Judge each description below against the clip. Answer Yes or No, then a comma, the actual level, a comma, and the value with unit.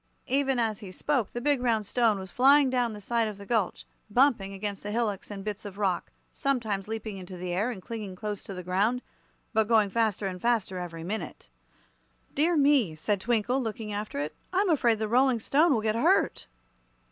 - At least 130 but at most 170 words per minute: No, fast, 205 wpm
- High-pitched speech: Yes, high, 215 Hz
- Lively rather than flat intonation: No, average, 3.9 semitones